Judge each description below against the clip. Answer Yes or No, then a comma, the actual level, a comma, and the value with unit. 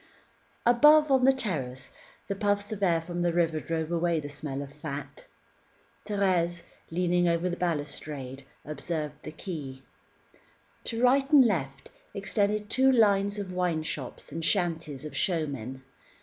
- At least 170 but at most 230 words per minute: No, average, 145 wpm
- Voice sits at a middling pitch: Yes, medium, 170 Hz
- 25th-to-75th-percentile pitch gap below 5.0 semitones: No, average, 5.3 semitones